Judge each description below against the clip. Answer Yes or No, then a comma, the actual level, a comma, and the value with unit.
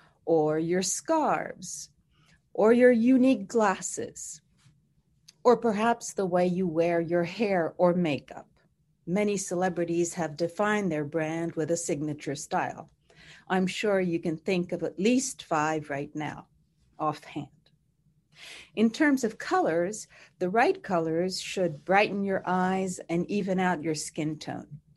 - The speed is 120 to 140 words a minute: Yes, slow, 135 wpm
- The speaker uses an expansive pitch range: No, average, 3.7 semitones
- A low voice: No, medium, 170 Hz